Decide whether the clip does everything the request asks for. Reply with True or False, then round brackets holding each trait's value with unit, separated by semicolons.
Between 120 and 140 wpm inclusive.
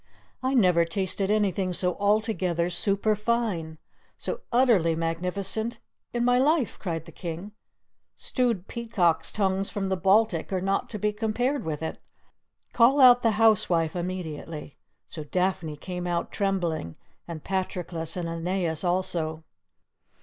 True (135 wpm)